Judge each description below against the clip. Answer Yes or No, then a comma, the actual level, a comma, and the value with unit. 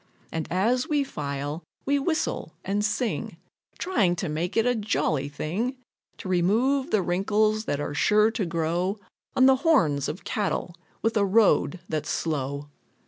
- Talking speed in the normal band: Yes, average, 155 wpm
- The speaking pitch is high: Yes, high, 195 Hz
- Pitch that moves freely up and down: Yes, wide, 6.1 semitones